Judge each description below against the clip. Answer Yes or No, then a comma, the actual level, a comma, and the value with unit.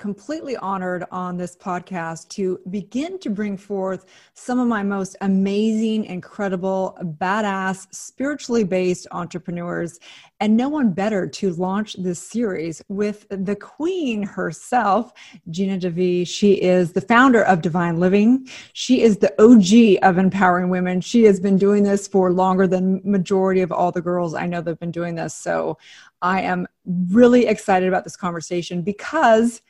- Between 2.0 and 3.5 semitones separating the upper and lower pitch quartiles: Yes, average, 2.9 semitones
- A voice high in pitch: Yes, high, 195 Hz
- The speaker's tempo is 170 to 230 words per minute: No, average, 155 wpm